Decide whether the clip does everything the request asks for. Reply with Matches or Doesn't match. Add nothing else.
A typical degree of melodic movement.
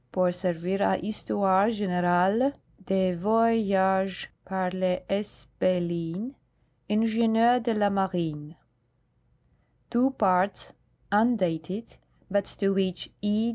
Matches